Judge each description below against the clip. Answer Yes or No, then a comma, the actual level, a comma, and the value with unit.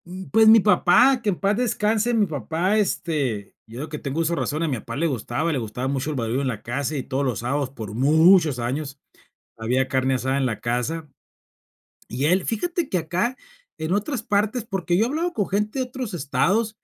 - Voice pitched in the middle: Yes, medium, 160 Hz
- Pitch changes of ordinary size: No, wide, 7.9 semitones